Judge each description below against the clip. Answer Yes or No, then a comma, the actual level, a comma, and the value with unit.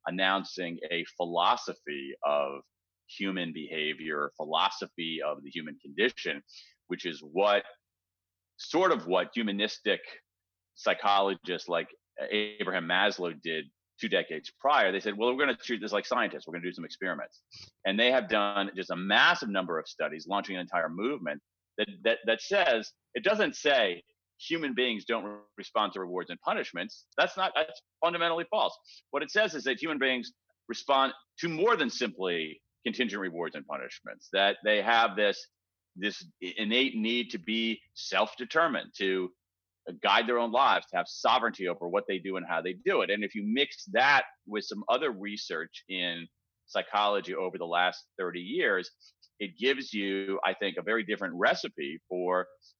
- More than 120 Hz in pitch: No, low, 100 Hz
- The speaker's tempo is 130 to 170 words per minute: Yes, average, 165 wpm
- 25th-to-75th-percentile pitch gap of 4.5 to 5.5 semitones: No, average, 4.1 semitones